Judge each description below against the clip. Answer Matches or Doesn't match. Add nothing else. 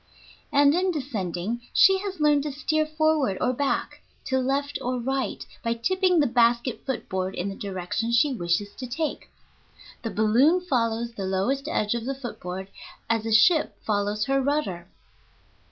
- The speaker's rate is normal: Matches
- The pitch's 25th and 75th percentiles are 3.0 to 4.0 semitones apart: Doesn't match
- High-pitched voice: Matches